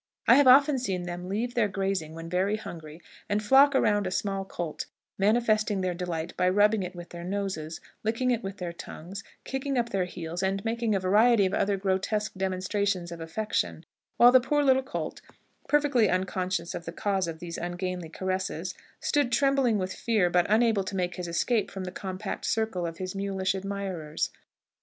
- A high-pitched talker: Yes, high, 195 Hz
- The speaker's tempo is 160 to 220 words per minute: Yes, average, 185 wpm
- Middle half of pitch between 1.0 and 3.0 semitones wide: No, average, 3.5 semitones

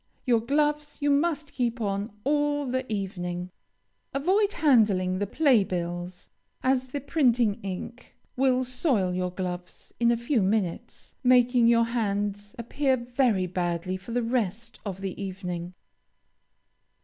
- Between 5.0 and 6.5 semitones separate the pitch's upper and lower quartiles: Yes, wide, 5.5 semitones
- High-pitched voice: Yes, high, 230 Hz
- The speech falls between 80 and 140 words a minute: Yes, slow, 135 wpm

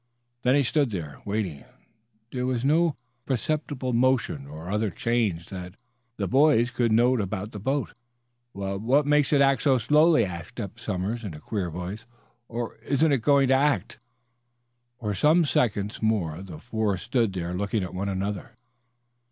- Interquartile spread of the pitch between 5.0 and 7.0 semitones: Yes, wide, 5.5 semitones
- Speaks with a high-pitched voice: No, low, 110 Hz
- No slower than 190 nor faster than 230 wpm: No, average, 165 wpm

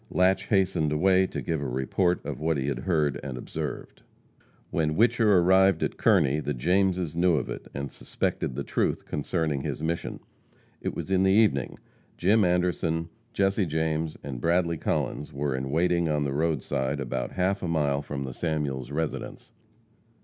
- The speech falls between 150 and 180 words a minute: Yes, average, 170 wpm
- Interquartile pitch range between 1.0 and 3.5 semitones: No, average, 4.3 semitones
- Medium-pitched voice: No, very low, 80 Hz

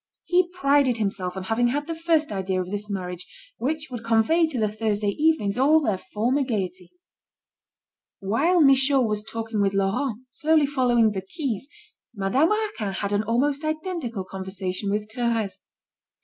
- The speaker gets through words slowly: No, average, 155 wpm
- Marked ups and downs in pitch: Yes, wide, 6.3 semitones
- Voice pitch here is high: Yes, high, 230 Hz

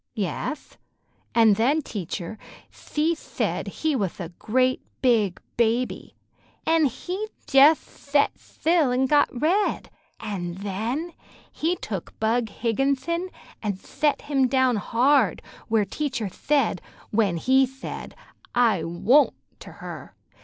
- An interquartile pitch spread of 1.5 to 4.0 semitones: No, wide, 5.6 semitones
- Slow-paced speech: Yes, slow, 120 wpm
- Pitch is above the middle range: Yes, very high, 250 Hz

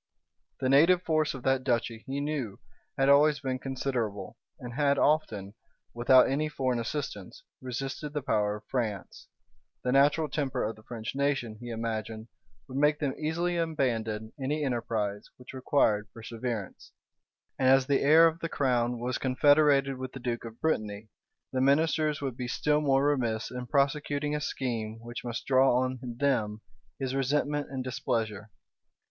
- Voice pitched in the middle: No, low, 130 Hz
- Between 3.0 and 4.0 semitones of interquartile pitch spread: Yes, average, 3.6 semitones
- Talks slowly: No, average, 160 wpm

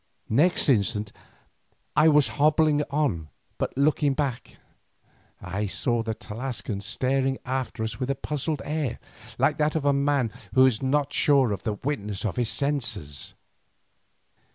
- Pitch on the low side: Yes, low, 130 Hz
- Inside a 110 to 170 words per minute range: Yes, average, 145 wpm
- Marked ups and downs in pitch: No, average, 4.6 semitones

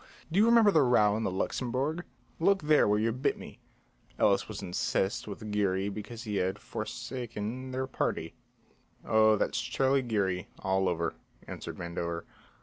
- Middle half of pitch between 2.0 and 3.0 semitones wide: No, average, 5.3 semitones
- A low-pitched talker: Yes, low, 110 Hz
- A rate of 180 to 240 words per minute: No, average, 155 wpm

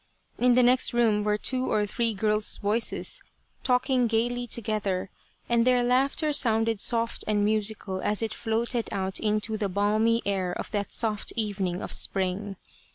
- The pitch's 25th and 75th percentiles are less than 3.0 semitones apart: Yes, narrow, 2.6 semitones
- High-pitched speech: Yes, high, 220 Hz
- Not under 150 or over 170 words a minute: Yes, average, 160 wpm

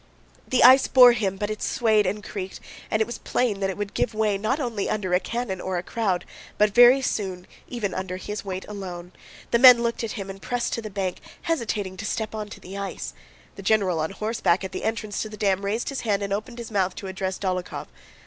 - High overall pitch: Yes, high, 205 Hz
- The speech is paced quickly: Yes, fast, 230 wpm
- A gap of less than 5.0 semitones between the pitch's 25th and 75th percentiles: Yes, average, 3.2 semitones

